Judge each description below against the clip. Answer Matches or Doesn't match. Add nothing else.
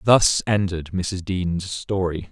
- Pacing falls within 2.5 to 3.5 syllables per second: Matches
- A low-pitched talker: Matches